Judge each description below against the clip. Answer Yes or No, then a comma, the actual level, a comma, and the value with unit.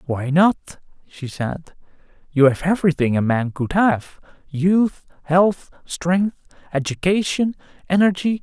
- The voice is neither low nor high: Yes, medium, 165 Hz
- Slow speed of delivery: Yes, slow, 105 wpm